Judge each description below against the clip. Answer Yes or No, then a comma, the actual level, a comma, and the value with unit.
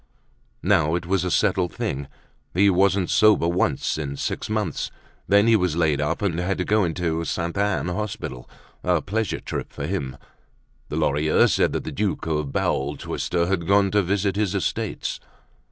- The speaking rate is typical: Yes, average, 180 wpm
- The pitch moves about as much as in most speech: Yes, average, 4.0 semitones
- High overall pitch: No, very low, 90 Hz